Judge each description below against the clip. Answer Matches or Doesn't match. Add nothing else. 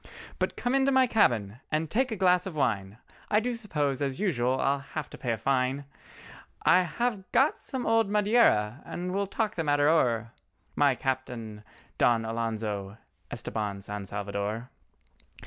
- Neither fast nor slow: Matches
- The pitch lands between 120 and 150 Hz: Matches